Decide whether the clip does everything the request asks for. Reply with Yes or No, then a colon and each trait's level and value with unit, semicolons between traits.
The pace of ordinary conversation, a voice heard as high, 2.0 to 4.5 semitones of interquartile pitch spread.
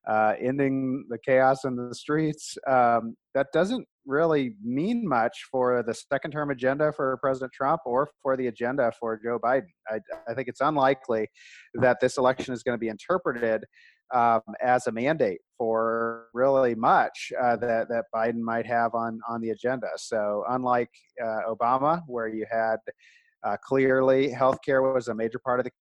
No: average, 175 wpm; low, 125 Hz; average, 2.8 semitones